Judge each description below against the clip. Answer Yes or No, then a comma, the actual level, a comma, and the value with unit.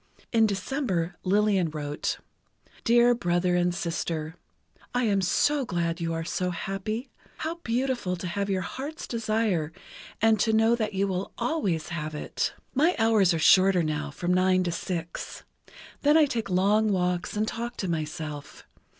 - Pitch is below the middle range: No, high, 190 Hz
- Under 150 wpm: No, average, 160 wpm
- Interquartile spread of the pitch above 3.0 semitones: Yes, average, 4.8 semitones